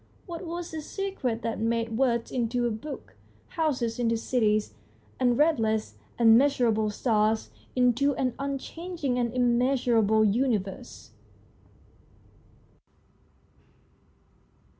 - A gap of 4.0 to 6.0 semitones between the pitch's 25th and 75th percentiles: No, average, 3.5 semitones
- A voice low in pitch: No, high, 245 Hz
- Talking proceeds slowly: Yes, slow, 95 wpm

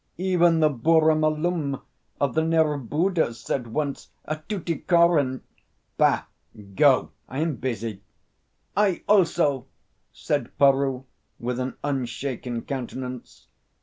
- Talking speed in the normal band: No, slow, 110 wpm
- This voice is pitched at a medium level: Yes, medium, 145 Hz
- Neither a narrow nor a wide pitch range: Yes, average, 4.2 semitones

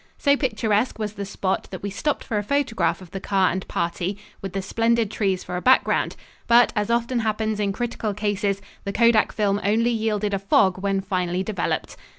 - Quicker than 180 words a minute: Yes, average, 195 wpm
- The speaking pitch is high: Yes, high, 205 Hz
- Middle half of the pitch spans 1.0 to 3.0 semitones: Yes, average, 2.7 semitones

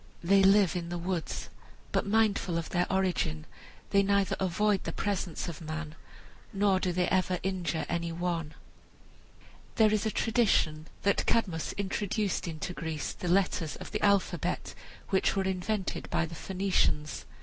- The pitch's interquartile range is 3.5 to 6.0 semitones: No, average, 2.9 semitones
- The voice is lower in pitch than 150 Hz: No, medium, 185 Hz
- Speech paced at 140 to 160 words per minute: Yes, average, 150 wpm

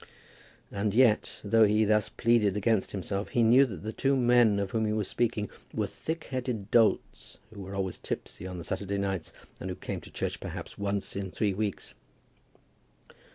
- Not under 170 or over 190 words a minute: Yes, average, 180 wpm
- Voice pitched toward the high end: No, low, 105 Hz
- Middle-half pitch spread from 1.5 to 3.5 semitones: Yes, narrow, 2.6 semitones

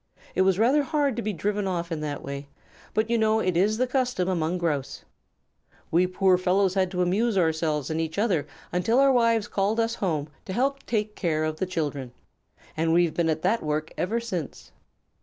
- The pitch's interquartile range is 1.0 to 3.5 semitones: No, wide, 5.4 semitones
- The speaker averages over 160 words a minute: Yes, average, 195 wpm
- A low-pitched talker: No, medium, 185 Hz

